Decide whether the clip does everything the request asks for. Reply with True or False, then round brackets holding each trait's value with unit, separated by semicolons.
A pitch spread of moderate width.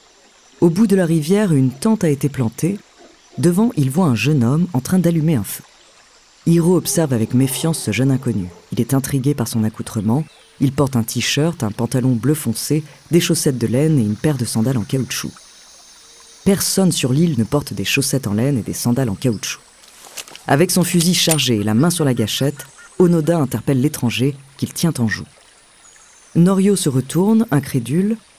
False (5.9 semitones)